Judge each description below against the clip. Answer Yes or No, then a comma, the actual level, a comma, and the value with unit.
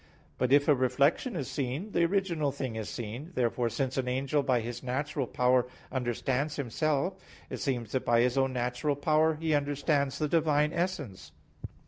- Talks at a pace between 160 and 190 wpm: Yes, average, 170 wpm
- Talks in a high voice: No, medium, 140 Hz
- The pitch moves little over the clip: No, average, 3.4 semitones